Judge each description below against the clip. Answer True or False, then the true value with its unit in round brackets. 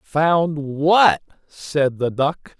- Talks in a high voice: False (150 Hz)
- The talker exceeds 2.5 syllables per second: False (2.2 syllables/s)